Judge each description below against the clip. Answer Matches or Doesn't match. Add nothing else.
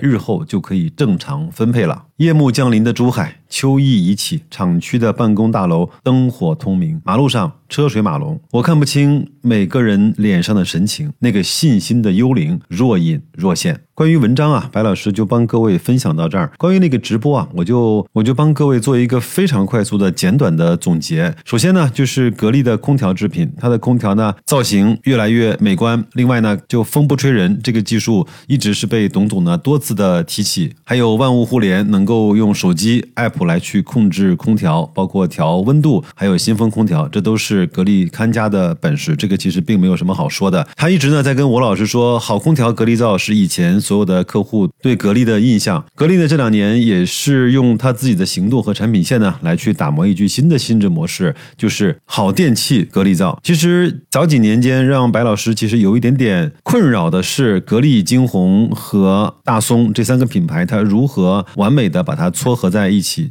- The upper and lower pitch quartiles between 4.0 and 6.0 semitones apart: Doesn't match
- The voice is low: Matches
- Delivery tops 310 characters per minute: Doesn't match